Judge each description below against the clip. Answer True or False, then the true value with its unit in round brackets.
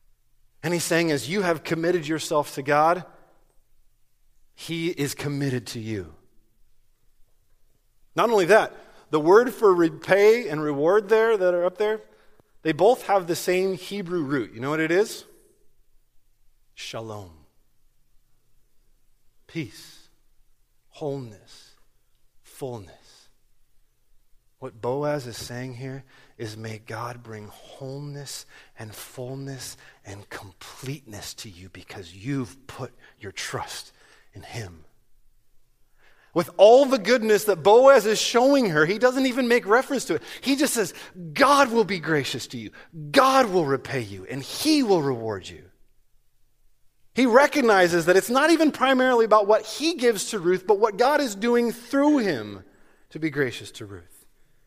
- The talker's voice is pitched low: False (155 Hz)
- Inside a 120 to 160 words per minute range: True (140 wpm)